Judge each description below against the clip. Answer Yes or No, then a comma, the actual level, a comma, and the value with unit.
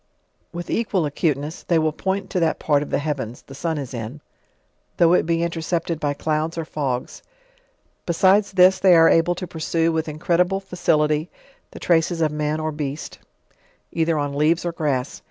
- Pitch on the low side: No, medium, 160 Hz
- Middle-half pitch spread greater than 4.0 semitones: No, narrow, 2.4 semitones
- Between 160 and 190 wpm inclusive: Yes, average, 180 wpm